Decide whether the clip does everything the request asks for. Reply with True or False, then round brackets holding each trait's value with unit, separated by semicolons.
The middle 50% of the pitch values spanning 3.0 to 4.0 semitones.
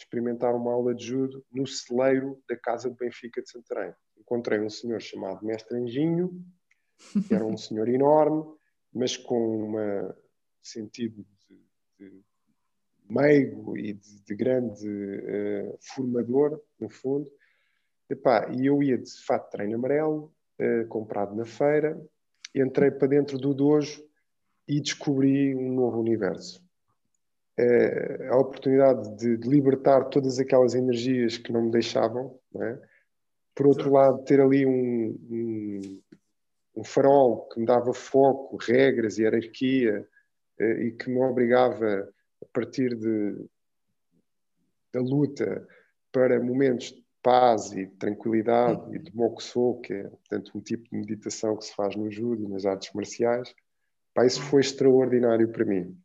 True (3.5 semitones)